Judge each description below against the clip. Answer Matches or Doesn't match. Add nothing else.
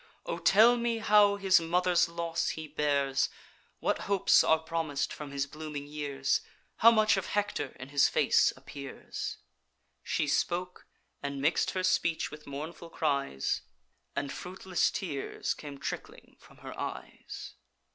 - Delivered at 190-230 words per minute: Doesn't match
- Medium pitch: Matches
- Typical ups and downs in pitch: Matches